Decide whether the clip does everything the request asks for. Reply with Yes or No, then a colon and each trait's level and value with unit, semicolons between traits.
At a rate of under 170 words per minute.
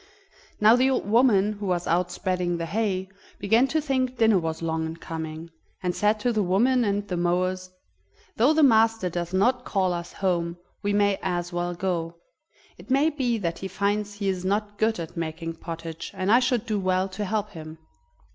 No: average, 195 wpm